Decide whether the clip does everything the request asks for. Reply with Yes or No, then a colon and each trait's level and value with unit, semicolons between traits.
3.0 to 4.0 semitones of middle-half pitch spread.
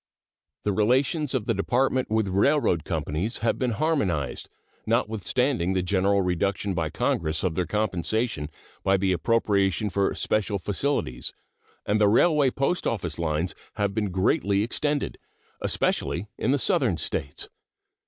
No: average, 4.7 semitones